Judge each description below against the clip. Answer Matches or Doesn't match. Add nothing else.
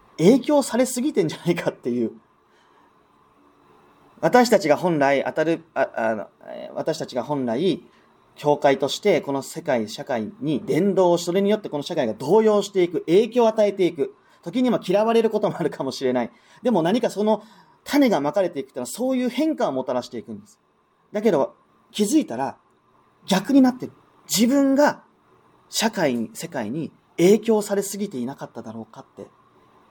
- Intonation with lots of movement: Matches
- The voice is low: Doesn't match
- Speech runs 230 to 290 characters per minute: Doesn't match